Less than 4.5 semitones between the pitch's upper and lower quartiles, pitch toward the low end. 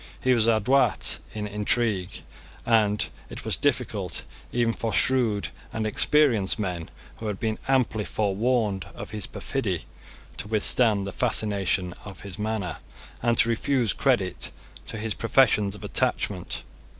Yes: average, 2.8 semitones; low, 110 Hz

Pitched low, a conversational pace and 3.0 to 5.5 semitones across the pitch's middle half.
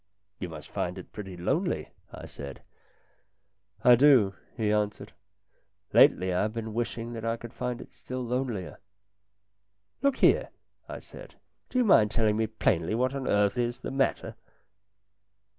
Yes: low, 110 Hz; average, 175 wpm; average, 3.5 semitones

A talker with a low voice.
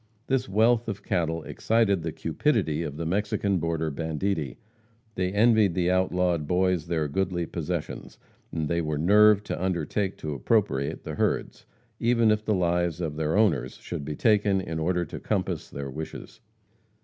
Yes: very low, 90 Hz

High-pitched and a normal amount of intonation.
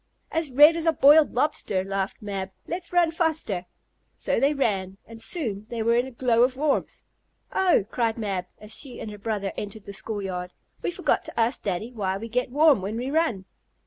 No: high, 230 Hz; wide, 6.4 semitones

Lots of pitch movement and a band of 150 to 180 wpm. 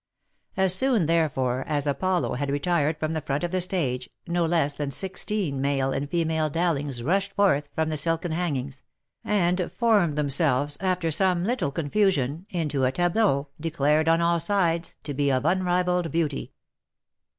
No: average, 3.9 semitones; average, 160 wpm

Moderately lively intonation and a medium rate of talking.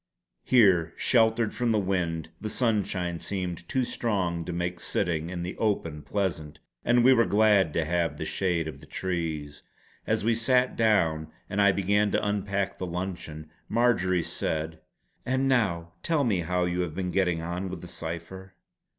Yes: average, 3.9 semitones; average, 170 wpm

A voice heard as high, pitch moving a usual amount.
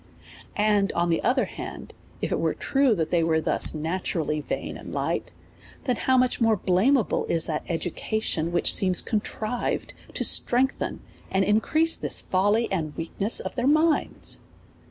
No: high, 205 Hz; wide, 6.5 semitones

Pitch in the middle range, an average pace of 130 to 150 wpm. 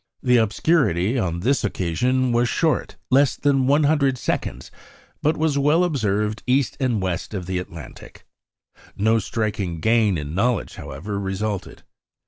No: low, 115 Hz; slow, 135 wpm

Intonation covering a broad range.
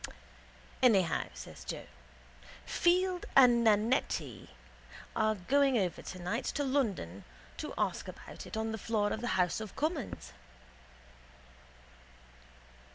Yes: wide, 5.9 semitones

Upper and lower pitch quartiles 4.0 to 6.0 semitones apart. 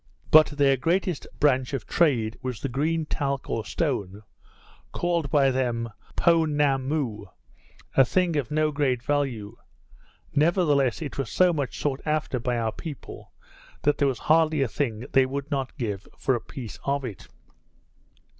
No: average, 3.5 semitones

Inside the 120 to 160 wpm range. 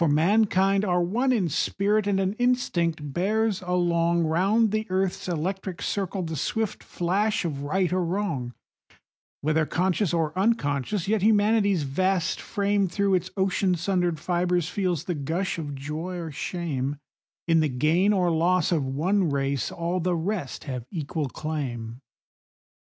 Yes: average, 150 wpm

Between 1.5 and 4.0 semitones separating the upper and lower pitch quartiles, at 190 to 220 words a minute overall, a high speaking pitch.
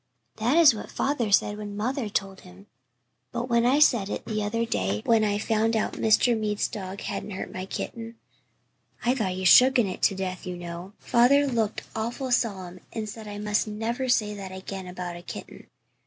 Yes: average, 3.5 semitones; average, 200 wpm; high, 210 Hz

